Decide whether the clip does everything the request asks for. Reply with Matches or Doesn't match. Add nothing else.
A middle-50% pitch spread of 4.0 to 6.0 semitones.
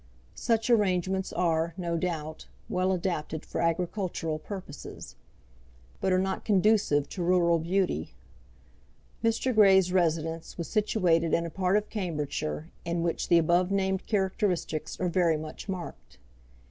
Doesn't match